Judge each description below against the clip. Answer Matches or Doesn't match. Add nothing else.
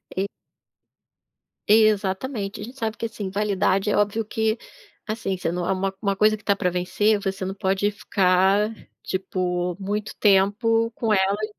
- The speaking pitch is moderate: Doesn't match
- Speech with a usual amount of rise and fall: Doesn't match